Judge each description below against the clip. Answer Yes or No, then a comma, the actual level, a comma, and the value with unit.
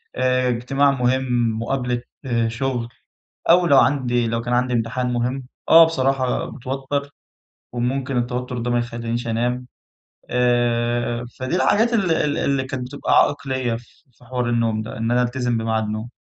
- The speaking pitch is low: Yes, low, 125 Hz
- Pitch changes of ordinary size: No, narrow, 1.8 semitones